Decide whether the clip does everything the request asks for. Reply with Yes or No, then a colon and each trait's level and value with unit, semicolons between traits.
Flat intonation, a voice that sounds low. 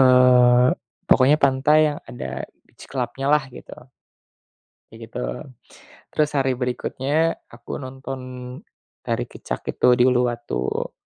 Yes: narrow, 1.7 semitones; low, 130 Hz